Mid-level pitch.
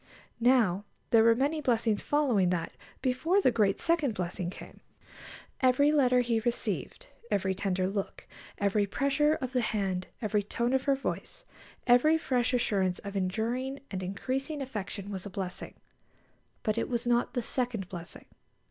No: high, 230 Hz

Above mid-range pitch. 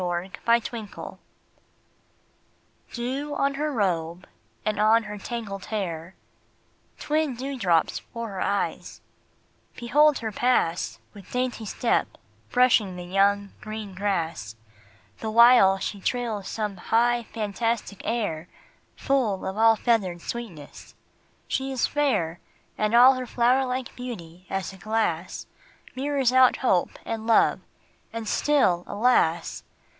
Yes: high, 220 Hz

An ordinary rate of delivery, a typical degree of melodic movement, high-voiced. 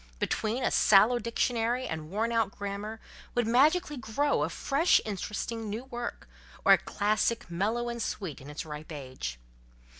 Yes: average, 155 wpm; average, 3.7 semitones; high, 220 Hz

